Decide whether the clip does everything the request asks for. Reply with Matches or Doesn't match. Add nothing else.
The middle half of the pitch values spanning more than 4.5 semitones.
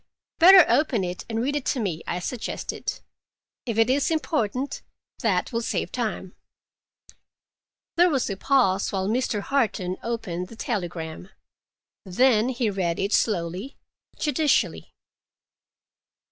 Matches